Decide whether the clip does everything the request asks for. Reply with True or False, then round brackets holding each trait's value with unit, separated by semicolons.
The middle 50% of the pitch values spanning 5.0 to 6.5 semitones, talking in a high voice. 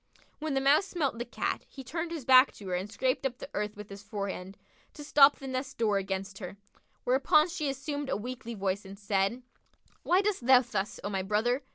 True (5.6 semitones; 245 Hz)